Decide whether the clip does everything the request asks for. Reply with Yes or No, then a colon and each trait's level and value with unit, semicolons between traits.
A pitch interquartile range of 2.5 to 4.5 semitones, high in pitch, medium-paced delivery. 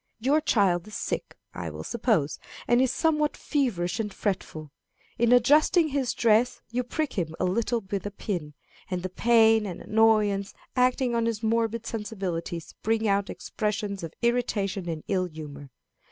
Yes: average, 4.2 semitones; high, 215 Hz; average, 160 wpm